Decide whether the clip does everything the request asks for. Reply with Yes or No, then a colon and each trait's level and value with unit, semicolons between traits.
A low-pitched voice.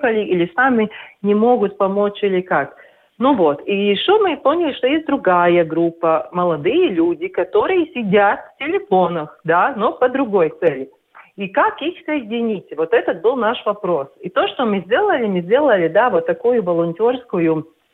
No: high, 220 Hz